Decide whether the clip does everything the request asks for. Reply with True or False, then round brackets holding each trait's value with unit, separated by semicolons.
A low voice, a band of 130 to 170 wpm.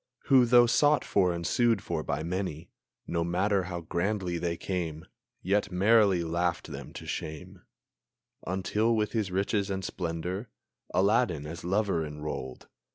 True (90 Hz; 145 wpm)